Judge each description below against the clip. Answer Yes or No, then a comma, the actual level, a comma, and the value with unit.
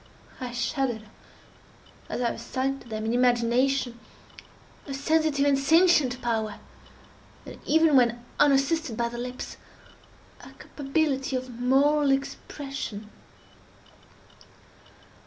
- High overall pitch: Yes, very high, 265 Hz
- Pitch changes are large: No, average, 2.8 semitones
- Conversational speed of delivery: No, slow, 100 wpm